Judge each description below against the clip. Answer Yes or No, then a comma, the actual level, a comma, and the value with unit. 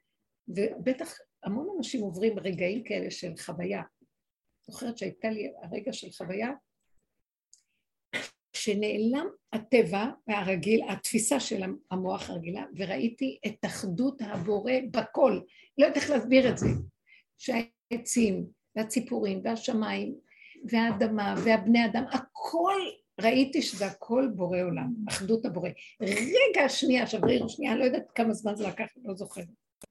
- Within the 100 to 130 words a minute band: Yes, average, 120 wpm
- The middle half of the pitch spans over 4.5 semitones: No, average, 4.0 semitones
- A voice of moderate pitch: No, high, 230 Hz